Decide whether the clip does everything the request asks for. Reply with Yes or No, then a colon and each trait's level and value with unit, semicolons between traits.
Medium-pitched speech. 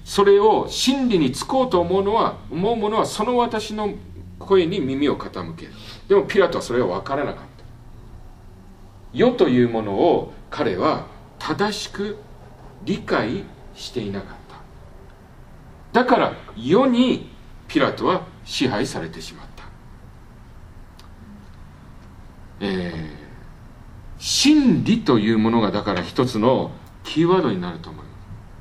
No: low, 115 Hz